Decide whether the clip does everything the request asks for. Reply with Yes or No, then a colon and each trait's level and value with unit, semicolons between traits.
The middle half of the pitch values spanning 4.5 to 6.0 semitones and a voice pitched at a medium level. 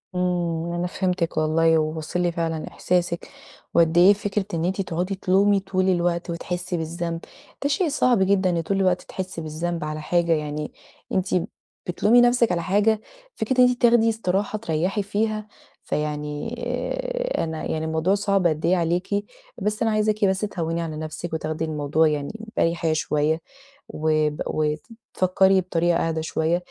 No: average, 3.6 semitones; medium, 175 Hz